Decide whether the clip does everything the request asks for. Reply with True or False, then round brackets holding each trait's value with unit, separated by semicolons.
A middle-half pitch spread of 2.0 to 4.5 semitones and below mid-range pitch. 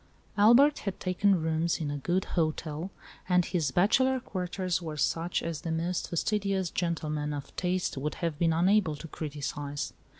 False (3.3 semitones; 170 Hz)